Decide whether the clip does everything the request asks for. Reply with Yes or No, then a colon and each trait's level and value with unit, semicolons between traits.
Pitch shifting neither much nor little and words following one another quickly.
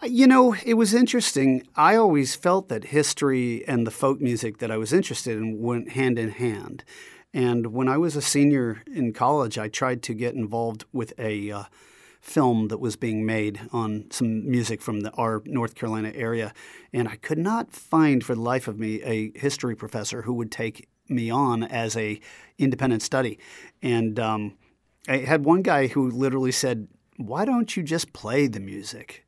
No: average, 4.0 semitones; average, 185 wpm